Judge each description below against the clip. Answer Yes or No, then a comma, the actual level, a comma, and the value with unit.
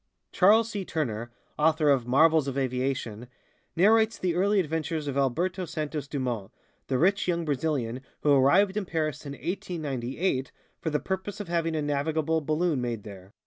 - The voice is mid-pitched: Yes, medium, 155 Hz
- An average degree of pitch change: Yes, average, 4.8 semitones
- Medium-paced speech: Yes, average, 160 wpm